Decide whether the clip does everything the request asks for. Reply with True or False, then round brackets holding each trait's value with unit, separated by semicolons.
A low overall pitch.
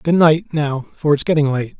False (150 Hz)